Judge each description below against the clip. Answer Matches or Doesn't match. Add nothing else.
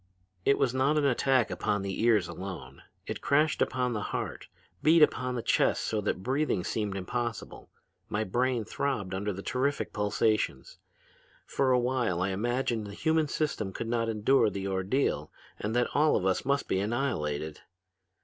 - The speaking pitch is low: Matches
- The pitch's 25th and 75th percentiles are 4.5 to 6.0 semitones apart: Matches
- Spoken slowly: Doesn't match